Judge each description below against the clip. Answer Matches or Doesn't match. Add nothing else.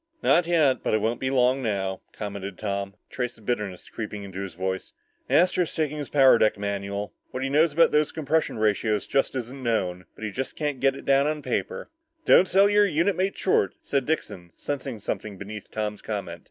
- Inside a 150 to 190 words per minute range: Doesn't match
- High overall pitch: Doesn't match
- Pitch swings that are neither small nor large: Doesn't match